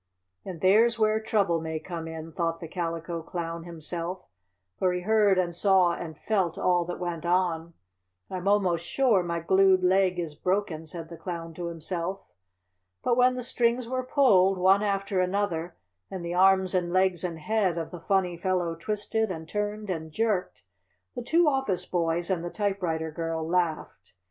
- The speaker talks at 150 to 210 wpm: Yes, average, 175 wpm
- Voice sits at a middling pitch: Yes, medium, 180 Hz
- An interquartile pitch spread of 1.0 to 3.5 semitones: Yes, average, 3.0 semitones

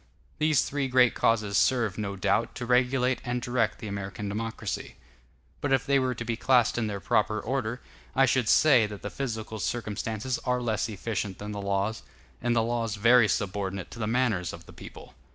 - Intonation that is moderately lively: Yes, average, 3.3 semitones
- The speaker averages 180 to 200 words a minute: Yes, average, 190 wpm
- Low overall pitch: Yes, low, 115 Hz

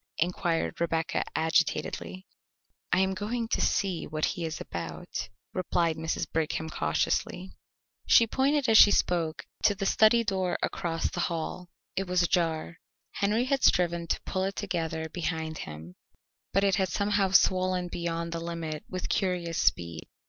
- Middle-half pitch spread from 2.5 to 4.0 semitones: Yes, average, 3.0 semitones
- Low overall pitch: No, medium, 175 Hz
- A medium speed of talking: Yes, average, 150 wpm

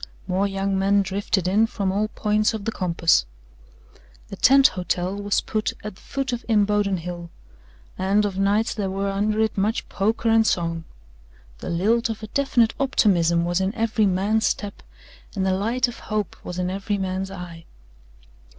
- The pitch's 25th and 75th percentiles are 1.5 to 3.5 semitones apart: Yes, narrow, 2.6 semitones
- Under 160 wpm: No, average, 175 wpm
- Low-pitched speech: No, high, 200 Hz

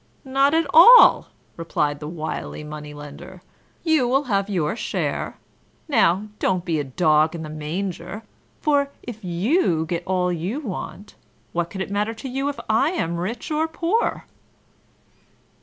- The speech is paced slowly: No, average, 155 wpm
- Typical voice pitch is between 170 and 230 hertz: Yes, high, 190 Hz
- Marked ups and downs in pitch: Yes, wide, 8.5 semitones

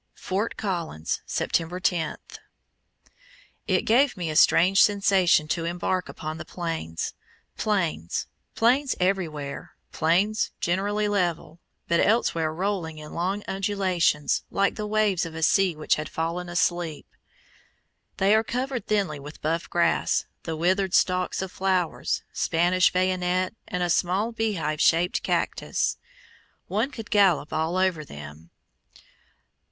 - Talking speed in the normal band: No, slow, 125 wpm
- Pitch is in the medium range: Yes, medium, 180 Hz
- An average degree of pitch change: Yes, average, 3.5 semitones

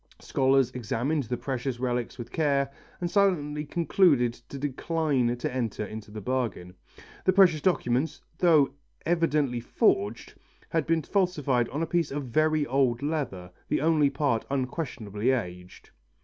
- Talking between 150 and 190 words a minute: No, average, 140 wpm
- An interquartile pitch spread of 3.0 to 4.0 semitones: No, average, 4.4 semitones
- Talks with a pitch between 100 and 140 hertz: Yes, low, 135 Hz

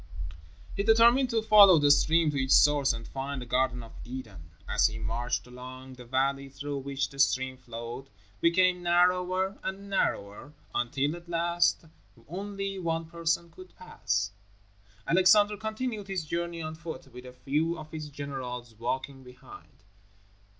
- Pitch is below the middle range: No, medium, 150 Hz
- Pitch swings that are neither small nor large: No, wide, 5.8 semitones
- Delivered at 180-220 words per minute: No, average, 150 wpm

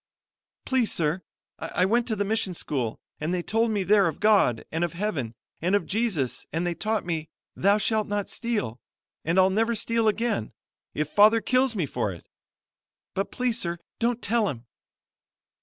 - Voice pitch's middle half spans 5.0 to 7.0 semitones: Yes, average, 5.3 semitones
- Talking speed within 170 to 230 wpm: Yes, average, 175 wpm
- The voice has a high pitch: Yes, high, 200 Hz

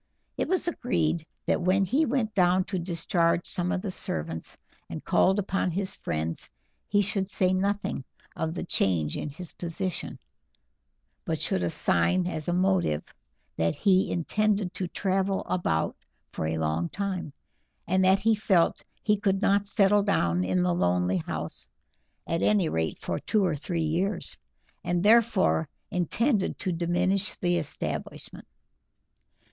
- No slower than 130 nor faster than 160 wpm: Yes, average, 150 wpm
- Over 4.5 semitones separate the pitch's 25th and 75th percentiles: No, average, 4.2 semitones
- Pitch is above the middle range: No, medium, 180 Hz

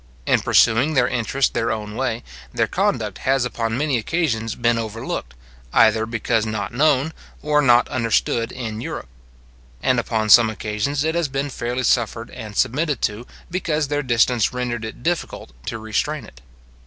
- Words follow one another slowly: No, average, 160 wpm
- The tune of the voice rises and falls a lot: No, average, 3.6 semitones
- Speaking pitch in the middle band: No, low, 120 Hz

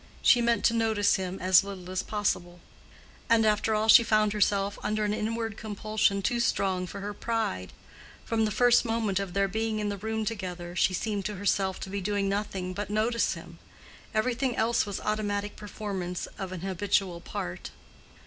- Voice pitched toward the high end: Yes, high, 205 Hz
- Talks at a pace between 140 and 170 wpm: No, average, 180 wpm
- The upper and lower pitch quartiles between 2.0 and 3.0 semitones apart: Yes, narrow, 2.4 semitones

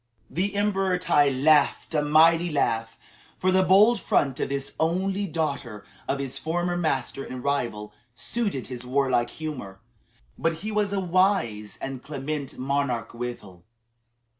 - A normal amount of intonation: No, wide, 5.9 semitones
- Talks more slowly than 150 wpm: Yes, average, 140 wpm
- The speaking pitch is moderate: Yes, medium, 145 Hz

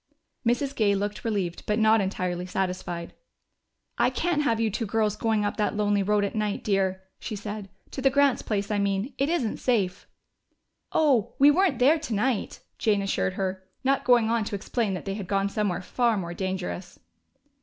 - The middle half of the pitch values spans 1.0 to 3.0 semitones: No, average, 3.4 semitones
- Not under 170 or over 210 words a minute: Yes, average, 185 wpm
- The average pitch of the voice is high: Yes, high, 210 Hz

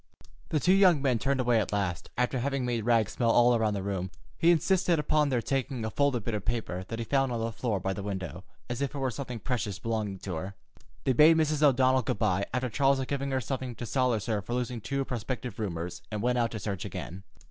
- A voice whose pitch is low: Yes, low, 120 Hz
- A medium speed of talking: No, fast, 245 wpm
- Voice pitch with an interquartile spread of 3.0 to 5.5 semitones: Yes, average, 4.3 semitones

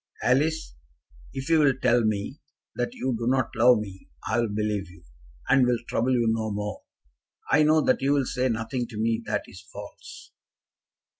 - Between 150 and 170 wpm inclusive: No, average, 180 wpm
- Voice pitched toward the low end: Yes, low, 120 Hz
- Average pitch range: Yes, average, 3.4 semitones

